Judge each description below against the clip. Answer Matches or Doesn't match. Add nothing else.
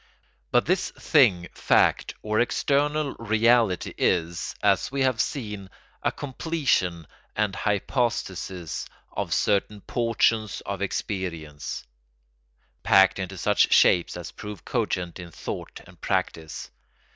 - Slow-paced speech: Matches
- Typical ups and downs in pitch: Matches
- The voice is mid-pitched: Doesn't match